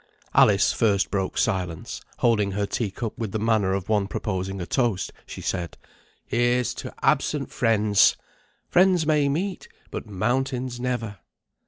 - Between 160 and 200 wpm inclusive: No, average, 145 wpm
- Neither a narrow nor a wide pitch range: Yes, average, 4.0 semitones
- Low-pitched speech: Yes, low, 110 Hz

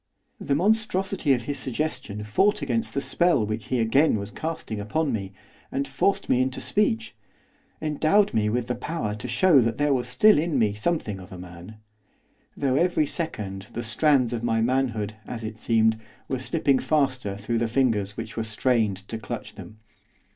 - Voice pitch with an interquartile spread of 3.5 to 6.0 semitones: Yes, average, 5.2 semitones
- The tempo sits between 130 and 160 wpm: No, average, 180 wpm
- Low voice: Yes, low, 120 Hz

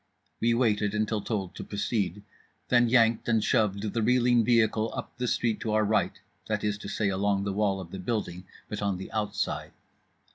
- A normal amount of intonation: No, narrow, 2.3 semitones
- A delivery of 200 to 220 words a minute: No, average, 190 wpm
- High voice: No, low, 105 Hz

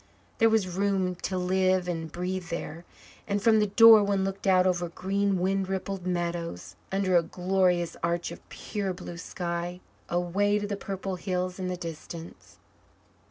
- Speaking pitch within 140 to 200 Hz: Yes, medium, 185 Hz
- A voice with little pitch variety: Yes, narrow, 1.9 semitones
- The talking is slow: No, average, 160 wpm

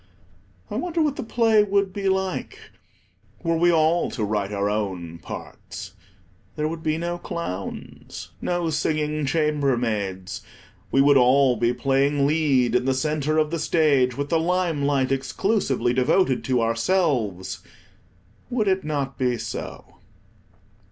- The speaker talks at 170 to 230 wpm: No, average, 140 wpm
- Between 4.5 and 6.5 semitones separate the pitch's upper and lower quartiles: Yes, average, 5.3 semitones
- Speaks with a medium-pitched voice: Yes, medium, 145 Hz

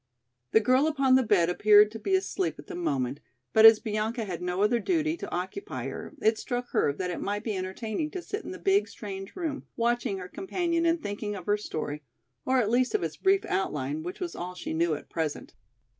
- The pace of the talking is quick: Yes, fast, 220 wpm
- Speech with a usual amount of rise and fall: No, wide, 8.6 semitones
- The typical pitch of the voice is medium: No, high, 220 Hz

